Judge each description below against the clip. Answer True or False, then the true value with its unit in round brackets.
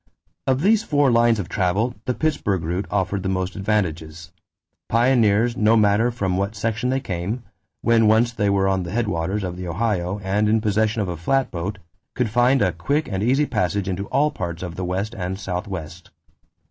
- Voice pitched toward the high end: False (100 Hz)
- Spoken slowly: False (185 wpm)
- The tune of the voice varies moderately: True (4.2 semitones)